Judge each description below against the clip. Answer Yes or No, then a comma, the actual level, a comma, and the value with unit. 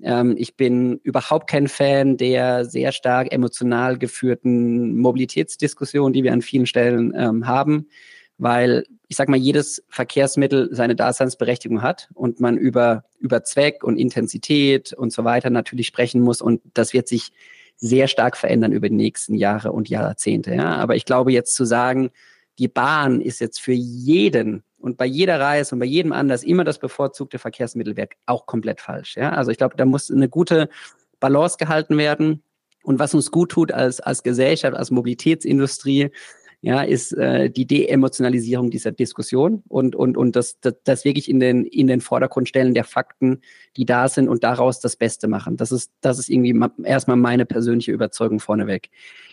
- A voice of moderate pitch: No, low, 125 Hz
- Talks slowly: No, average, 170 wpm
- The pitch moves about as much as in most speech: No, narrow, 2.3 semitones